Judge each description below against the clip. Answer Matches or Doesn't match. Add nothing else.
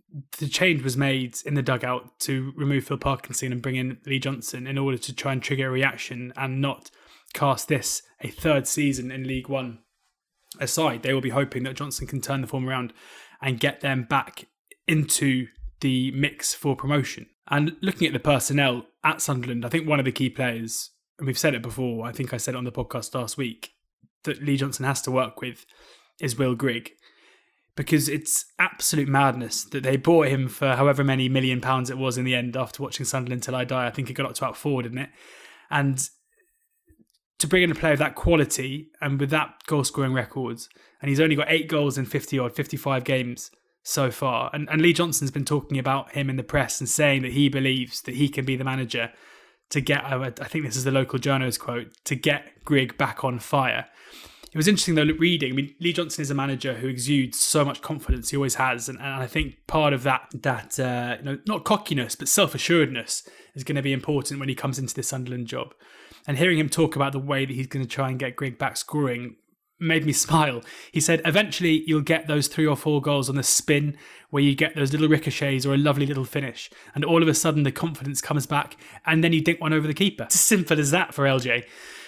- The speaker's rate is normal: Doesn't match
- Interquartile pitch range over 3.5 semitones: Doesn't match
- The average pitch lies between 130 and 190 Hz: Matches